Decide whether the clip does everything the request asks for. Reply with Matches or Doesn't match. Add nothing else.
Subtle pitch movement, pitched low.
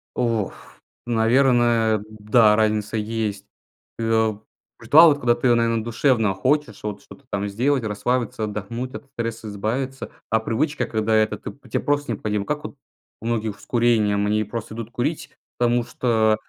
Matches